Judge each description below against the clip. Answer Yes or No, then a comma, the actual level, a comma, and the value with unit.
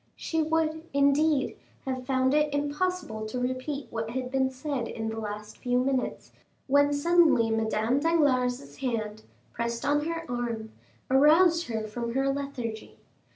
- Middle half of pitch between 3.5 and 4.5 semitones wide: Yes, average, 4.0 semitones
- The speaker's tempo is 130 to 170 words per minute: Yes, average, 140 wpm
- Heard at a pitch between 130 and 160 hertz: No, very high, 265 Hz